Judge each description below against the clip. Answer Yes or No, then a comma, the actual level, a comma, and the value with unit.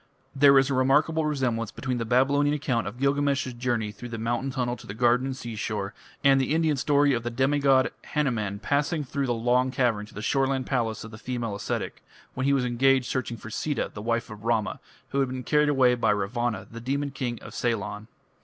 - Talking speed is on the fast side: Yes, fast, 210 wpm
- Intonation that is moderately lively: Yes, average, 3.0 semitones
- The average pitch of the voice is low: Yes, low, 125 Hz